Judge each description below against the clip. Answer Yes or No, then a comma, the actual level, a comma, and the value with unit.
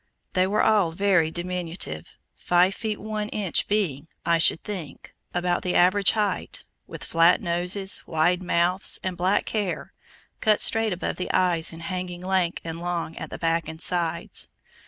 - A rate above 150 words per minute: Yes, average, 160 wpm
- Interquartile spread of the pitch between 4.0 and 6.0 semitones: No, narrow, 2.6 semitones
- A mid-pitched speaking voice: Yes, medium, 180 Hz